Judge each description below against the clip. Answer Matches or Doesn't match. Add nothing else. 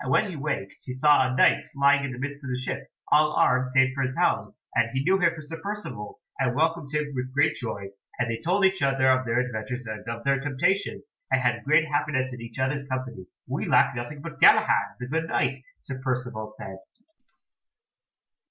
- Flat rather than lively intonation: Doesn't match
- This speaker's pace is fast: Matches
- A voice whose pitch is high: Doesn't match